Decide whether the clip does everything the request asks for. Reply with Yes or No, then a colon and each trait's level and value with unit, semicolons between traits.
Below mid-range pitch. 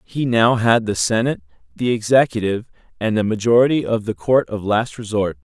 Yes: low, 115 Hz